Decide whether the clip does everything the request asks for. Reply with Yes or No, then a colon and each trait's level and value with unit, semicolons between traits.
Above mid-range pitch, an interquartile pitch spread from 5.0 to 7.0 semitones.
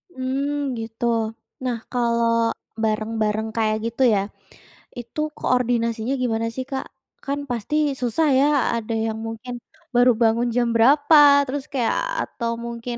No: high, 240 Hz; average, 2.7 semitones